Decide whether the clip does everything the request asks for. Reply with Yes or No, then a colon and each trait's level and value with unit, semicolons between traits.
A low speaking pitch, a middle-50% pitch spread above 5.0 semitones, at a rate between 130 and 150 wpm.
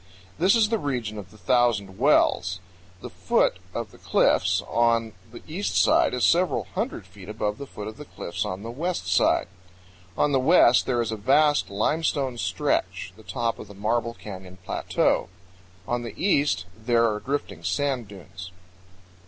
No: low, 115 Hz; wide, 5.4 semitones; average, 170 wpm